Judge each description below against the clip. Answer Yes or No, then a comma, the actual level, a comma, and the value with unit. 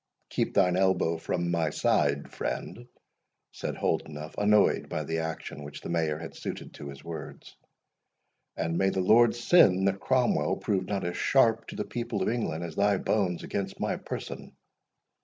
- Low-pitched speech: Yes, very low, 90 Hz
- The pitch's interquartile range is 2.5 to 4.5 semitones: Yes, average, 4.2 semitones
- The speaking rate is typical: Yes, average, 170 wpm